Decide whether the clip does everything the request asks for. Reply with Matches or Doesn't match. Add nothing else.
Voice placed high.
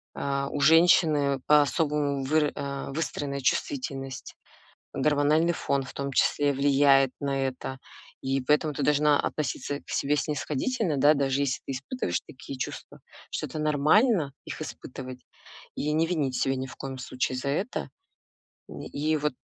Doesn't match